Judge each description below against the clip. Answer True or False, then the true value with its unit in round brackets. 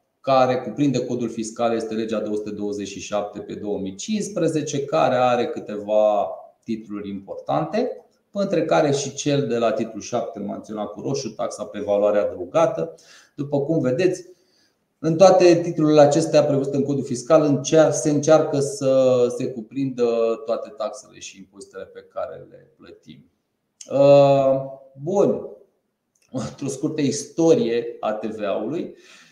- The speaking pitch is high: False (135 Hz)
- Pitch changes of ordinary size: False (5.8 semitones)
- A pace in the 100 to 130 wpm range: True (120 wpm)